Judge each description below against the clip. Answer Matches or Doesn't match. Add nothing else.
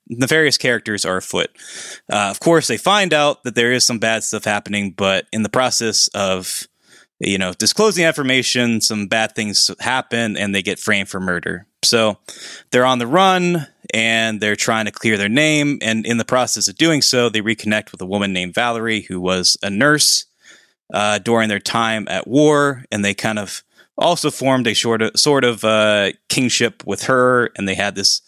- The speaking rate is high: Doesn't match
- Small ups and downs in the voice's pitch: Doesn't match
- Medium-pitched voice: Doesn't match